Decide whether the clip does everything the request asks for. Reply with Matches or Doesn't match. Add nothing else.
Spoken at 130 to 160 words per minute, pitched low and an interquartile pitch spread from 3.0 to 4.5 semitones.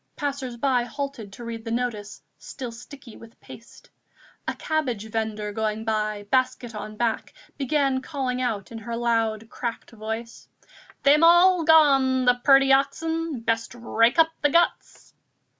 Doesn't match